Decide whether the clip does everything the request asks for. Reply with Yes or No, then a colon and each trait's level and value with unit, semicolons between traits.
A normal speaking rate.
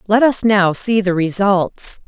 Yes: average, 175 wpm